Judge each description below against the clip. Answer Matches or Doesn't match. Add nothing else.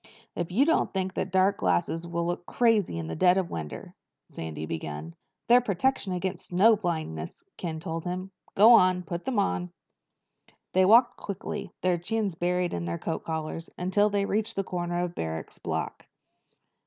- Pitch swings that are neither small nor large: Matches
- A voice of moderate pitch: Matches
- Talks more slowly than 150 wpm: Doesn't match